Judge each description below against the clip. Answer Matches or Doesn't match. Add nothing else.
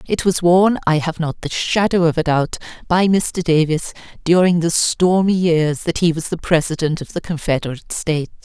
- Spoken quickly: Doesn't match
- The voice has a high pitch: Doesn't match